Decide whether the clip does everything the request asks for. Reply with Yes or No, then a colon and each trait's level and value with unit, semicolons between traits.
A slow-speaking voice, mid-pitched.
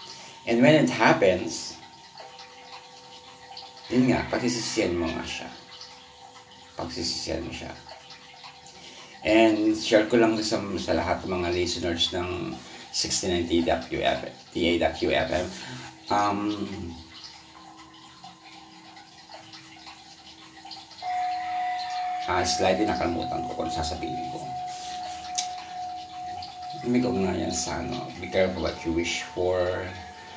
No: slow, 90 wpm; low, 105 Hz